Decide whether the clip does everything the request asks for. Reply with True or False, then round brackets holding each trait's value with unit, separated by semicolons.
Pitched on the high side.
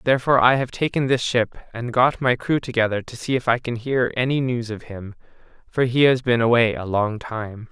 False (120 Hz)